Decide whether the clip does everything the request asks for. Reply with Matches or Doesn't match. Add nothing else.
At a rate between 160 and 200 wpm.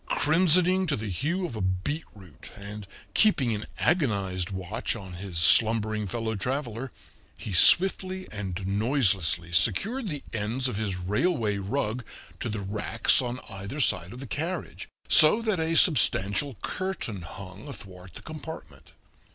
Doesn't match